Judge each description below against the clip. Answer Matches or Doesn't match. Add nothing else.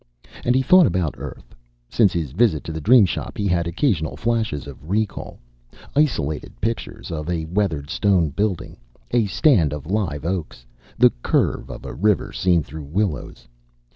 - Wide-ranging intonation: Matches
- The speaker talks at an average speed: Matches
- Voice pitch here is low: Matches